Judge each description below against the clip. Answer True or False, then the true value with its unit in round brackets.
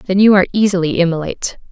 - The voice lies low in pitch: False (185 Hz)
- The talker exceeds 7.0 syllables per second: True (7.3 syllables/s)